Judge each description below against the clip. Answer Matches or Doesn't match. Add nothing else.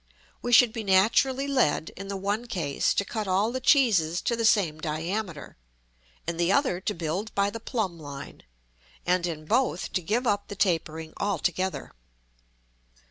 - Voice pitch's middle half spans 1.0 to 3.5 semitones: Doesn't match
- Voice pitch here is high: Matches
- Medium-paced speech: Matches